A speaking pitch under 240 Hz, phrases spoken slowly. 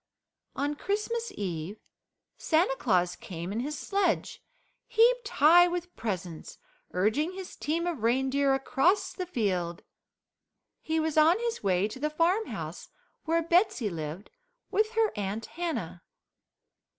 No: very high, 300 Hz; slow, 125 wpm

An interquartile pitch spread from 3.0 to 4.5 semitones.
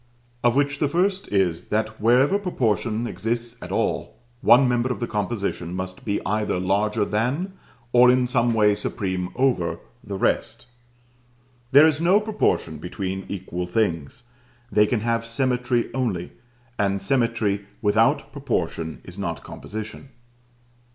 Yes: average, 4.1 semitones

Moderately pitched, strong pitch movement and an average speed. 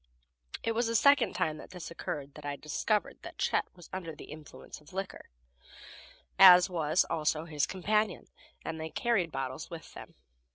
No: medium, 170 Hz; average, 4.1 semitones; average, 170 wpm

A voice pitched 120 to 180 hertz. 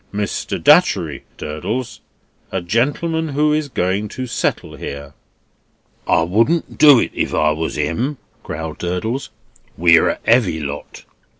No: low, 105 Hz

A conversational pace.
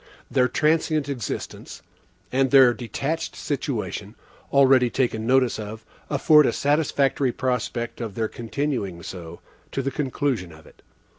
No: slow, 130 wpm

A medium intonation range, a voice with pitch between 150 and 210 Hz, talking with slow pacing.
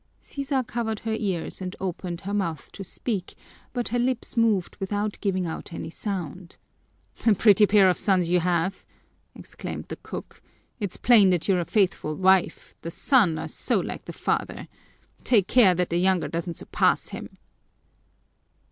No: average, 3.6 semitones; high, 190 Hz; average, 165 wpm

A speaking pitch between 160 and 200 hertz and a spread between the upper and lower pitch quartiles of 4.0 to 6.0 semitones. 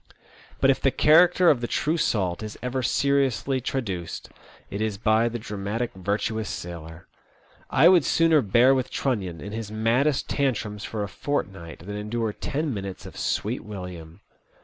No: low, 110 Hz; average, 5.1 semitones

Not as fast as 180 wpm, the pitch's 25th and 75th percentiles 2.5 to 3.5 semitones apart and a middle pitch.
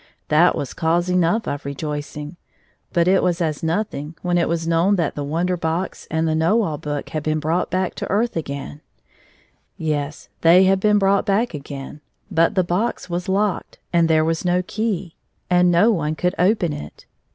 No: average, 190 wpm; average, 3.1 semitones; medium, 170 Hz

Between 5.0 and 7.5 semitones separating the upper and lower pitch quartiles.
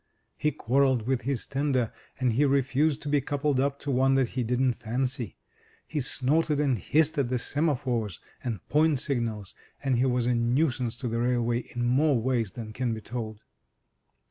No: average, 2.8 semitones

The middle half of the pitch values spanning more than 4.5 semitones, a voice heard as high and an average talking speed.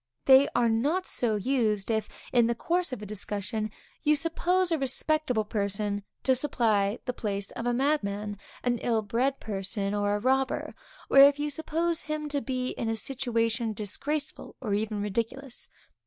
Yes: average, 4.9 semitones; high, 240 Hz; average, 170 wpm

